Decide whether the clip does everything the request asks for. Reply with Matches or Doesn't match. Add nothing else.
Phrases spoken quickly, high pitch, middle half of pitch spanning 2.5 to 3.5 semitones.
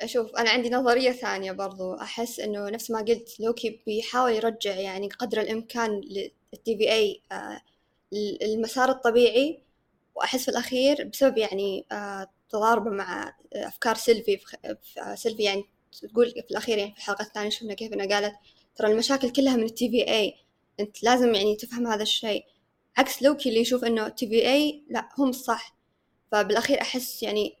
Matches